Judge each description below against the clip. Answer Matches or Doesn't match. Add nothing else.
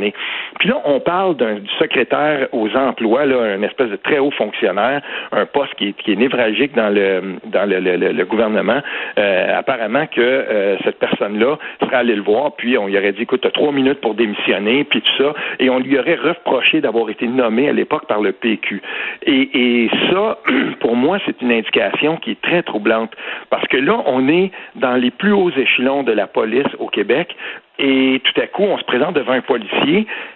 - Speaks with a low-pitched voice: Matches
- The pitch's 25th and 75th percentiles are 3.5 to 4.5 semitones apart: Matches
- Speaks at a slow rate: Doesn't match